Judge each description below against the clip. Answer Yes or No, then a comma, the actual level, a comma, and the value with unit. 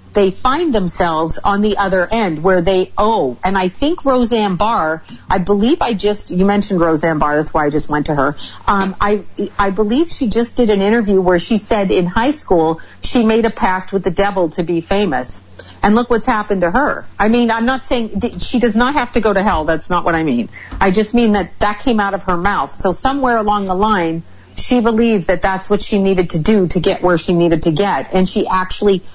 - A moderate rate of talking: No, fast, 235 wpm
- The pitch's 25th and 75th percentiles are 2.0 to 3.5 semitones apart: No, average, 3.9 semitones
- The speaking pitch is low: No, high, 200 Hz